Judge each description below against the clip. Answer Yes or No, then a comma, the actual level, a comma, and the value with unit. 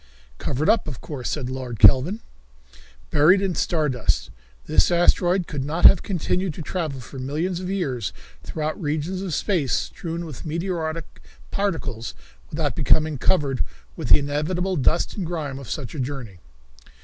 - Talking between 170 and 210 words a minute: No, average, 155 wpm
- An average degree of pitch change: Yes, average, 4.5 semitones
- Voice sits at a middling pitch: Yes, medium, 155 Hz